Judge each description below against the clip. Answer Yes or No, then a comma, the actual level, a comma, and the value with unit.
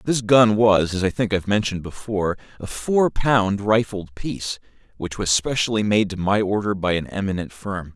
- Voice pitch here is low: Yes, low, 105 Hz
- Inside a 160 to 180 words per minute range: No, average, 195 wpm